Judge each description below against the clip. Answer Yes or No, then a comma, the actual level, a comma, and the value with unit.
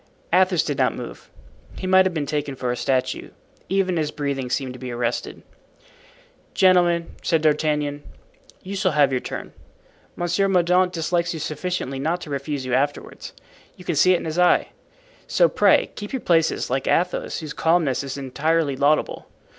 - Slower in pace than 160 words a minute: No, average, 170 wpm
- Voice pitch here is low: No, medium, 155 Hz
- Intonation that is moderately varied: Yes, average, 4.4 semitones